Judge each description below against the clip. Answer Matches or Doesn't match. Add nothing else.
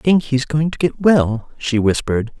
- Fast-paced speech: Matches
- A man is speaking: Matches